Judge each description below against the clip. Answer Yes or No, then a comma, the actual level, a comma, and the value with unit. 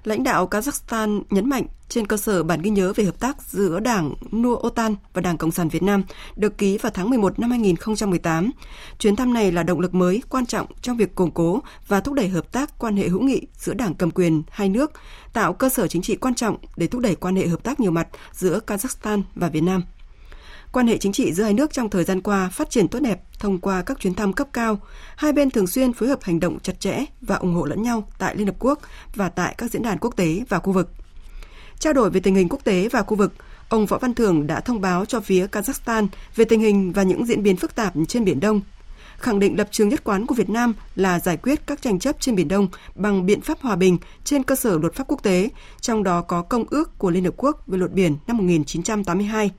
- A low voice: No, high, 205 Hz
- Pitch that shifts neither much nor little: Yes, average, 4.5 semitones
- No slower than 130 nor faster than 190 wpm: No, fast, 250 wpm